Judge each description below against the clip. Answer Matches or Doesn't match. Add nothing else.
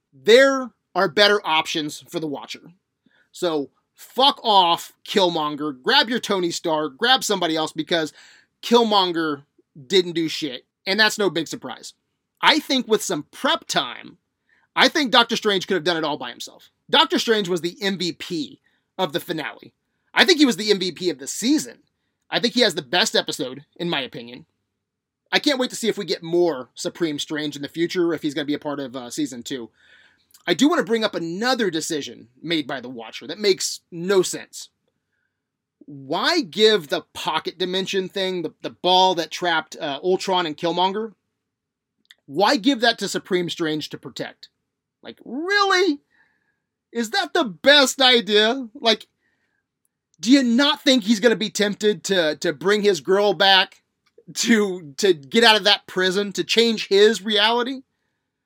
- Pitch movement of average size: Doesn't match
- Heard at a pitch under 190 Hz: Doesn't match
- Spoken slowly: Doesn't match